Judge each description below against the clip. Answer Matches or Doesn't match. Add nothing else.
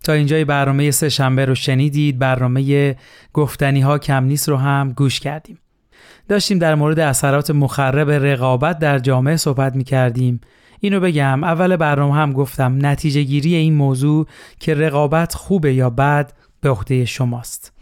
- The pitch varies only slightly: Matches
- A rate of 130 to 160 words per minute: Matches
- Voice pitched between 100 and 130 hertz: Doesn't match